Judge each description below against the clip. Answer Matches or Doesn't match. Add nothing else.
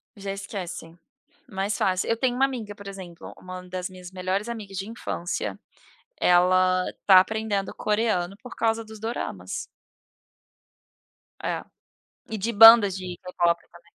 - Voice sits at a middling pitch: Doesn't match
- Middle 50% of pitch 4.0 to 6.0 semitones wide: Doesn't match